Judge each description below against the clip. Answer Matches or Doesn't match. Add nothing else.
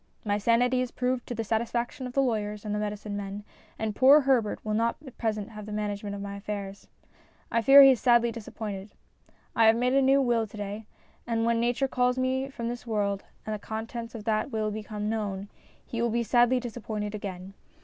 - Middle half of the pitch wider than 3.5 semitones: Doesn't match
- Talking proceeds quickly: Matches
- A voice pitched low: Doesn't match